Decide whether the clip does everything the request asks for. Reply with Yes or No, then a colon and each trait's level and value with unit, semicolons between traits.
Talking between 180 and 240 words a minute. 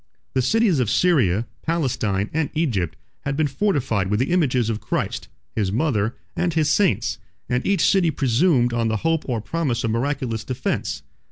No: average, 170 wpm